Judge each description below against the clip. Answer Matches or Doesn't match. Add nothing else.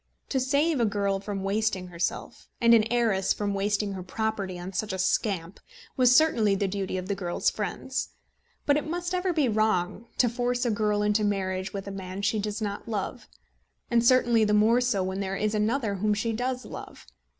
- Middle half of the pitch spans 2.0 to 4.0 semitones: Matches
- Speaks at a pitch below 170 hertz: Doesn't match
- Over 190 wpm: Matches